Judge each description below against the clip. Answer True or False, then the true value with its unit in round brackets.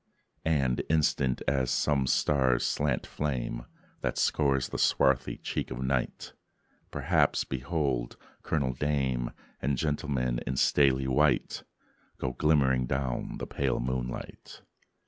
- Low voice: True (65 Hz)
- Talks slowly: True (115 wpm)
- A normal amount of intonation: False (2.2 semitones)